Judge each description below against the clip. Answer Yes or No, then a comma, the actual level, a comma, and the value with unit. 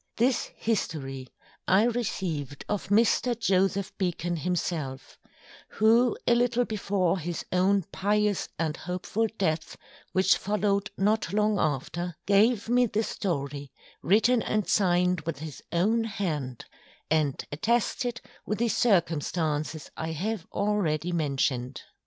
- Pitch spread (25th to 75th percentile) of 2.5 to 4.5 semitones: No, average, 5.1 semitones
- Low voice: No, high, 190 Hz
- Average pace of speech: No, slow, 120 wpm